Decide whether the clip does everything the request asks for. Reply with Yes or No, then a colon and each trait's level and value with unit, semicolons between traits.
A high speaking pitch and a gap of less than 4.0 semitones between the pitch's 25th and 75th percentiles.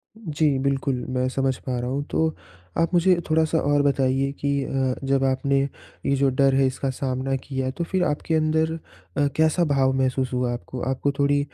No: low, 135 Hz; average, 2.8 semitones